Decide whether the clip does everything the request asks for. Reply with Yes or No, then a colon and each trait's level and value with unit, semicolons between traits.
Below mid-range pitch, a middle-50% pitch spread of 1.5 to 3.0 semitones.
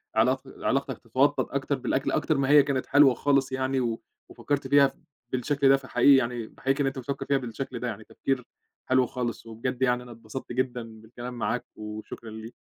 Yes: low, 130 Hz; narrow, 2.4 semitones